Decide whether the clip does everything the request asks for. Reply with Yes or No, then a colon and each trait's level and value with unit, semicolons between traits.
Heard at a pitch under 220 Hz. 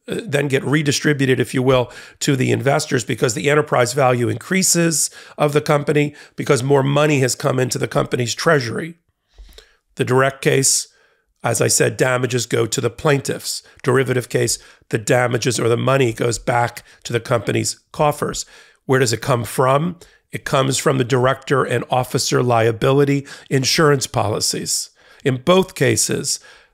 Yes: low, 135 Hz